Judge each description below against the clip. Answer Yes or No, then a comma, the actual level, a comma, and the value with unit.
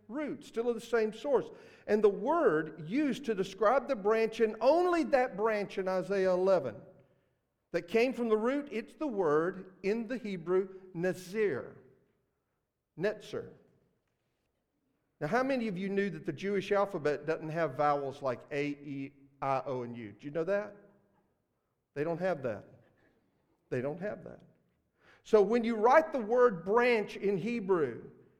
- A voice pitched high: Yes, high, 205 Hz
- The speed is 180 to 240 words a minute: No, average, 160 wpm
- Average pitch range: No, wide, 5.8 semitones